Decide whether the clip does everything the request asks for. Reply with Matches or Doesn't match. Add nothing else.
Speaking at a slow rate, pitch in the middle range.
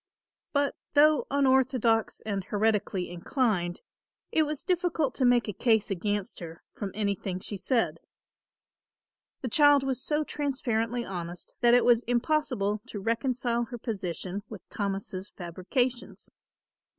Doesn't match